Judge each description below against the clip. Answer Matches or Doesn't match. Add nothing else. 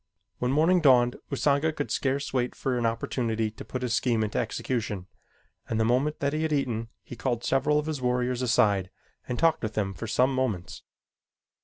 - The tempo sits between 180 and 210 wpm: Matches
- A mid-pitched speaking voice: Doesn't match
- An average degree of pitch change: Matches